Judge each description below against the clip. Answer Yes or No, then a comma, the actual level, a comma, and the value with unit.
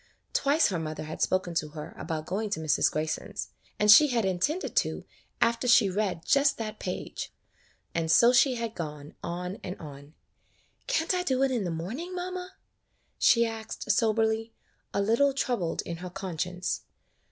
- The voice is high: Yes, high, 210 Hz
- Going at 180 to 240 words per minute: No, average, 170 wpm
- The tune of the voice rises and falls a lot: Yes, wide, 6.5 semitones